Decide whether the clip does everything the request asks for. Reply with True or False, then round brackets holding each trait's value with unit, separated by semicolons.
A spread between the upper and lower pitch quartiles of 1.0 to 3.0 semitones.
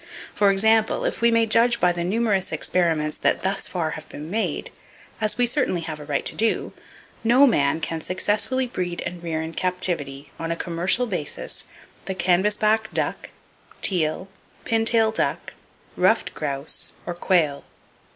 False (5.1 semitones)